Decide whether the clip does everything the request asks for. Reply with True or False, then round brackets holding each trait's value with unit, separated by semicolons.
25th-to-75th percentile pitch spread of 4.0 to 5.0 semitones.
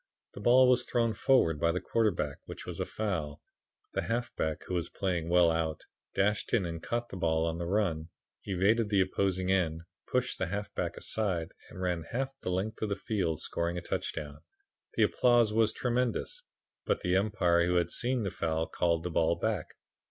True (4.6 semitones)